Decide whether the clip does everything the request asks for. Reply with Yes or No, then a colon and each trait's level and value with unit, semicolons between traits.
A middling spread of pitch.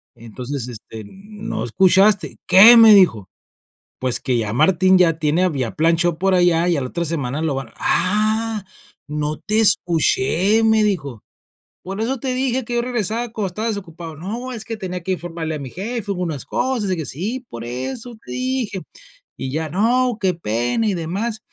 No: wide, 6.3 semitones